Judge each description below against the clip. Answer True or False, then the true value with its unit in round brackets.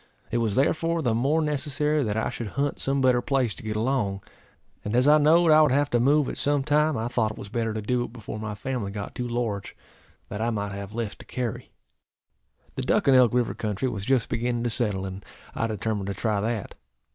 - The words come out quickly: True (230 wpm)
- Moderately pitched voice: False (120 Hz)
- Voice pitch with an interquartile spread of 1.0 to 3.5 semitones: False (4.1 semitones)